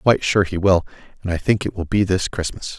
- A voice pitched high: No, very low, 95 Hz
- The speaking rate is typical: No, fast, 280 wpm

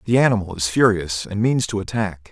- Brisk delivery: Yes, fast, 210 wpm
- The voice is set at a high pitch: No, low, 105 Hz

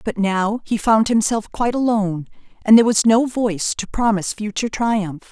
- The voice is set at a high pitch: Yes, high, 215 Hz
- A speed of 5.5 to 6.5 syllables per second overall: Yes, 5.6 syllables/s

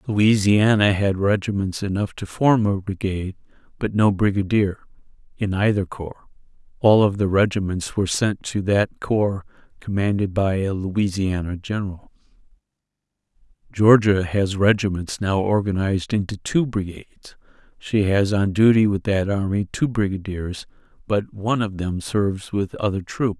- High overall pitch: No, low, 100 Hz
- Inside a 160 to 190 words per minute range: No, slow, 135 wpm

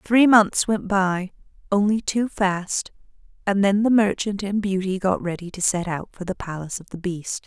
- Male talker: No, female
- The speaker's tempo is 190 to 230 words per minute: Yes, average, 195 wpm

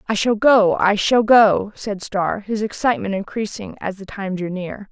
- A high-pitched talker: Yes, high, 195 Hz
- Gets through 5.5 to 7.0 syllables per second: No, 4.5 syllables/s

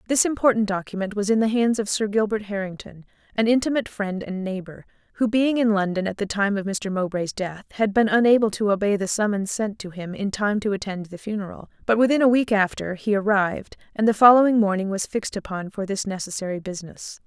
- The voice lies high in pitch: Yes, high, 205 Hz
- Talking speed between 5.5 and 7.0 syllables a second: Yes, 6.0 syllables/s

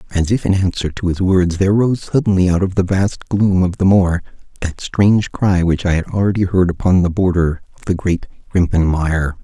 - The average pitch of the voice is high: No, very low, 90 Hz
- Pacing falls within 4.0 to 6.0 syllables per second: Yes, 5.3 syllables/s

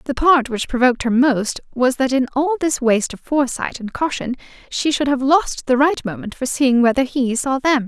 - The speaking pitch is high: Yes, very high, 260 Hz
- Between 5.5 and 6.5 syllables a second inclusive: No, 5.2 syllables/s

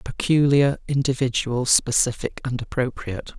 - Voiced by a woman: No, male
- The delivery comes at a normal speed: No, slow, 90 wpm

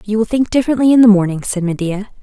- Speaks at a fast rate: Yes, fast, 240 wpm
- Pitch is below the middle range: No, high, 215 Hz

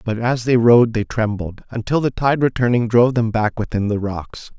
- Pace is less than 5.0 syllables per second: No, 5.3 syllables/s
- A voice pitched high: No, low, 115 Hz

